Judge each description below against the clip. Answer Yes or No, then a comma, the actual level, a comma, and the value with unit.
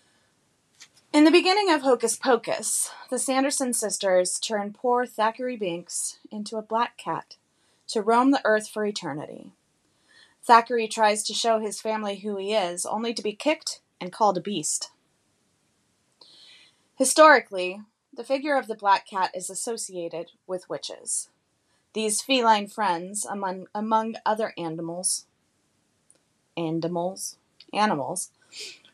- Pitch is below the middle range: No, high, 215 Hz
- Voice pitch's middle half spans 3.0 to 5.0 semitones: Yes, average, 4.3 semitones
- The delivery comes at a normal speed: No, slow, 125 wpm